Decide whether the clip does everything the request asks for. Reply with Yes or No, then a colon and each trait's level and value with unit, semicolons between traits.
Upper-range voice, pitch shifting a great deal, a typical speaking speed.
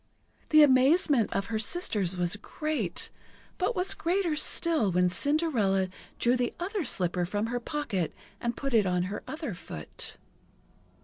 Yes: high, 240 Hz; wide, 8.3 semitones; average, 145 wpm